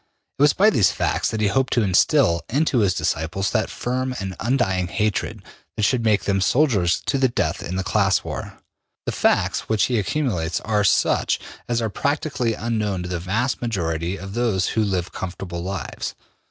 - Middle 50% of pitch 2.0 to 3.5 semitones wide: No, average, 4.7 semitones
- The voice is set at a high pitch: No, low, 105 Hz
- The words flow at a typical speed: Yes, average, 185 wpm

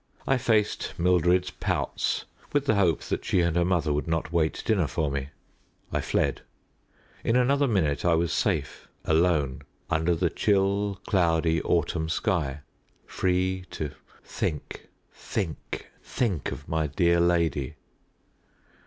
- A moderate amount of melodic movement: Yes, average, 3.2 semitones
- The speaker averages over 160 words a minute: No, slow, 135 wpm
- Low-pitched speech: Yes, very low, 85 Hz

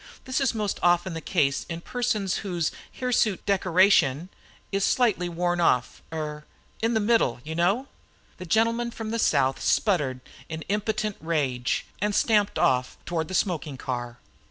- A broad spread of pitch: Yes, wide, 5.7 semitones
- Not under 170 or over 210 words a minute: No, average, 155 wpm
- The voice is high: No, medium, 180 Hz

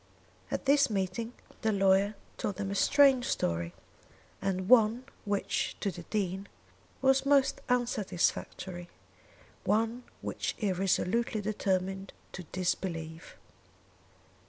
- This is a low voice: No, high, 200 Hz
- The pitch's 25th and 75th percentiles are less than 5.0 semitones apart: Yes, average, 4.0 semitones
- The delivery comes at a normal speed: No, slow, 110 wpm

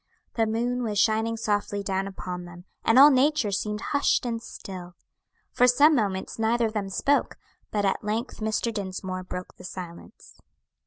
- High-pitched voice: Yes, high, 215 Hz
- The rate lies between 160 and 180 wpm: Yes, average, 165 wpm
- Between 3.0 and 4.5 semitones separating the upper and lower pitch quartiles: Yes, average, 3.6 semitones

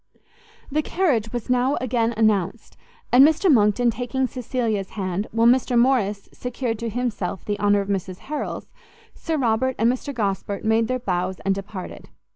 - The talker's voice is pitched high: Yes, high, 230 Hz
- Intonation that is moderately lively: Yes, average, 3.8 semitones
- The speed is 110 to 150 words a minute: No, average, 160 wpm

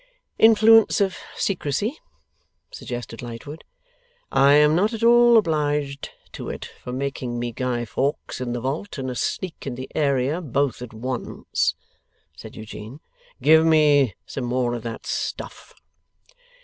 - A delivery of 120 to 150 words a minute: Yes, average, 140 wpm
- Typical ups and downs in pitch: Yes, average, 4.8 semitones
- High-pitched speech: No, medium, 140 Hz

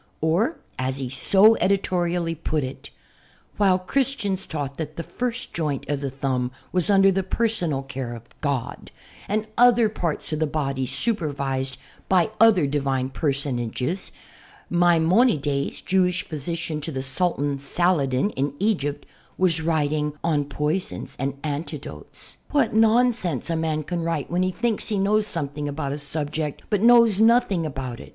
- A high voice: No, medium, 160 Hz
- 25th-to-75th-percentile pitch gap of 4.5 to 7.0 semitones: Yes, wide, 5.5 semitones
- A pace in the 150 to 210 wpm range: Yes, average, 155 wpm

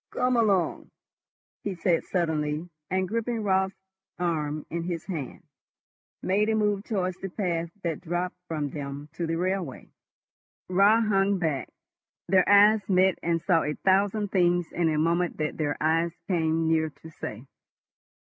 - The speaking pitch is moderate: Yes, medium, 175 Hz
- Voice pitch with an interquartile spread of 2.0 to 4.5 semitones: Yes, average, 3.3 semitones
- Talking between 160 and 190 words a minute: No, average, 150 wpm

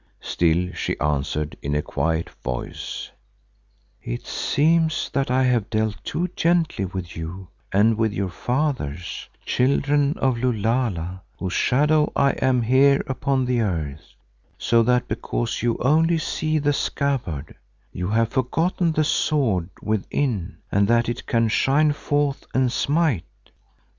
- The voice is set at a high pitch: No, low, 120 Hz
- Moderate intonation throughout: No, wide, 7.1 semitones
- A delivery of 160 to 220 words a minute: No, slow, 135 wpm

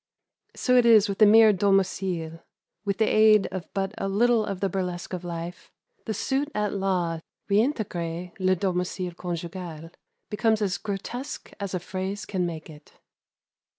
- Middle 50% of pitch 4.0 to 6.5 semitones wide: No, average, 3.0 semitones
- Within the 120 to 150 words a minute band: No, average, 160 wpm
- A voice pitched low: No, high, 195 Hz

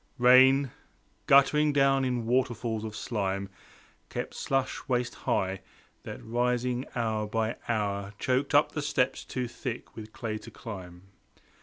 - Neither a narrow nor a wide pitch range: Yes, average, 3.2 semitones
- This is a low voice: Yes, low, 120 Hz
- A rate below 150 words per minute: Yes, slow, 135 wpm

